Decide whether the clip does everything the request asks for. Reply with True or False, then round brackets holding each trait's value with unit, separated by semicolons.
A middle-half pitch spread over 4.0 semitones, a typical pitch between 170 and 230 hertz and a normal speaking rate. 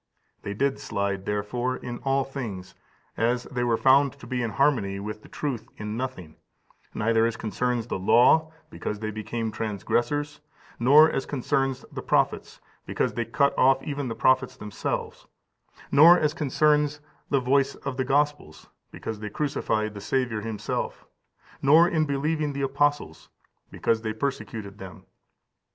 False (4.5 semitones; 125 Hz; 150 wpm)